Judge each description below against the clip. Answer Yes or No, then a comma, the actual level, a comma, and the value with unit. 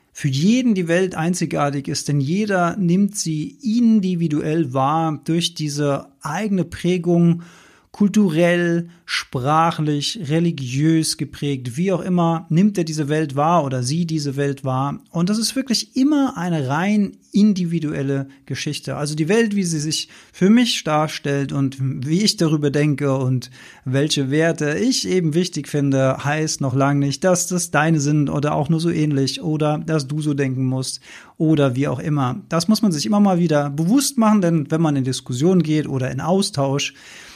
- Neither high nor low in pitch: Yes, medium, 155 Hz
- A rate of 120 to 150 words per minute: No, average, 165 wpm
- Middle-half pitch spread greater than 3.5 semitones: Yes, average, 4.0 semitones